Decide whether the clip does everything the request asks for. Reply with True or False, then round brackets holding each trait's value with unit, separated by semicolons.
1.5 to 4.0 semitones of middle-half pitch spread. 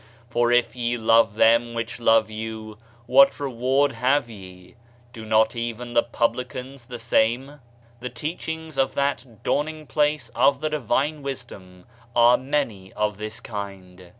True (3.6 semitones)